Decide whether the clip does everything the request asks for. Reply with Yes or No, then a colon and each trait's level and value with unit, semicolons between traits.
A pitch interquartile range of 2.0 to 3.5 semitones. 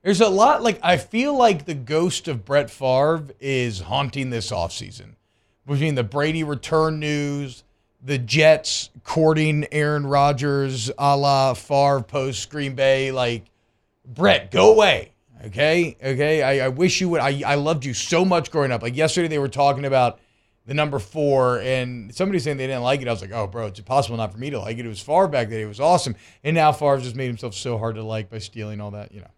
No: average, 4.3 semitones